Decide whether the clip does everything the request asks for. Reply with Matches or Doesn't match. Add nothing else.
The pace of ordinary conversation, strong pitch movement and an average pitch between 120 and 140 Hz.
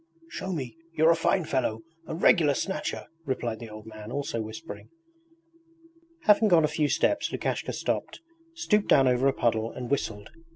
Matches